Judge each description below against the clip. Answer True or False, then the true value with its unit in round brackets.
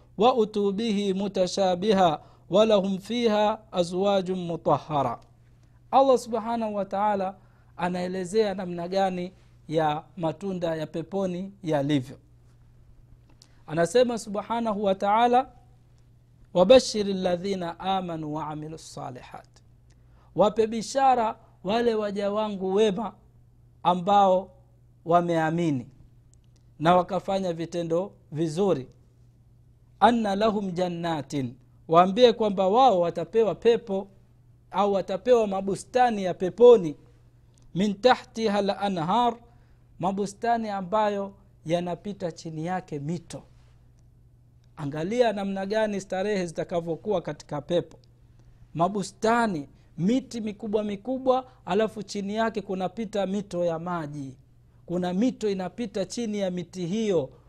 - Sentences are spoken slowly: True (90 wpm)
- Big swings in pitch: True (6.6 semitones)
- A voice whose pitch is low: False (180 Hz)